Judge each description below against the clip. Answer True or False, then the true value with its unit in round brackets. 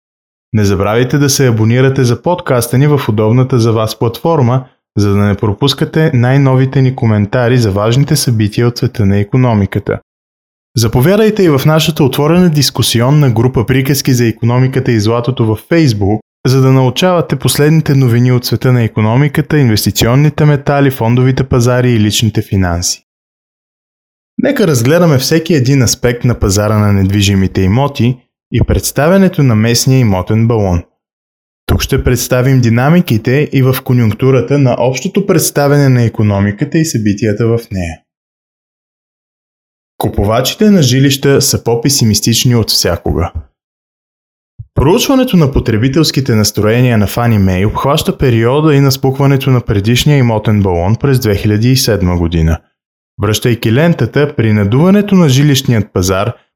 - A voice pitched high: False (125 Hz)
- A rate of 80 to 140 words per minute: True (130 wpm)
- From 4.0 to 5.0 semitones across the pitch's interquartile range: True (4.5 semitones)